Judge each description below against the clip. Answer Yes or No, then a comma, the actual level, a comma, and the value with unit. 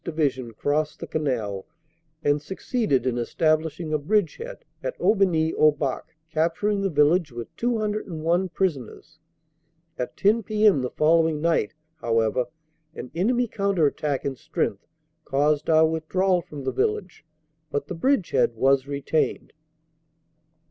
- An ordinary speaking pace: No, slow, 125 wpm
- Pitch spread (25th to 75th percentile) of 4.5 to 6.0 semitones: Yes, average, 5.2 semitones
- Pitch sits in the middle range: Yes, medium, 155 Hz